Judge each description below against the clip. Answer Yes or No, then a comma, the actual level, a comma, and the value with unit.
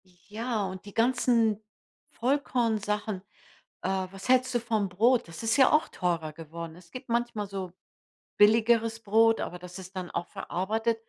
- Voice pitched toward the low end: No, high, 215 Hz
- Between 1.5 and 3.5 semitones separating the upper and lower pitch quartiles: No, average, 4.0 semitones